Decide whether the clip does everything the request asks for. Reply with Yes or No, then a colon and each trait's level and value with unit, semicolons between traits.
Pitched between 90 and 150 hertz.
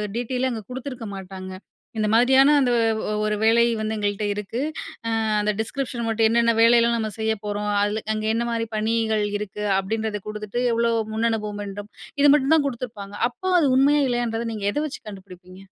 No: high, 225 Hz